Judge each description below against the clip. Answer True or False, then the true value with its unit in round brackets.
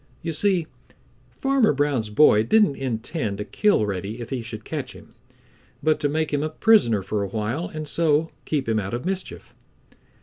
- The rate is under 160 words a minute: False (180 wpm)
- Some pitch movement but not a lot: False (6.7 semitones)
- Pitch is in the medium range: True (145 Hz)